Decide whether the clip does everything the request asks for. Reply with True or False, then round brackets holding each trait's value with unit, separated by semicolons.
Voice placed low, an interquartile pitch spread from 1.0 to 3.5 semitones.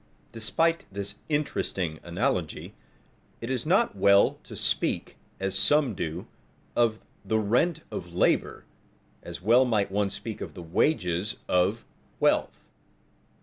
False (105 Hz; 5.5 semitones)